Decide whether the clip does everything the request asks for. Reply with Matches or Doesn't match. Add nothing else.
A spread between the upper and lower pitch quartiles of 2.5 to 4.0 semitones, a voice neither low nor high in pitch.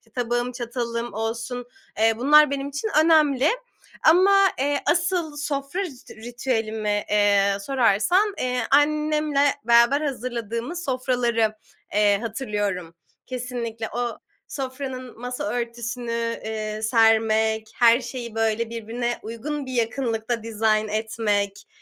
Doesn't match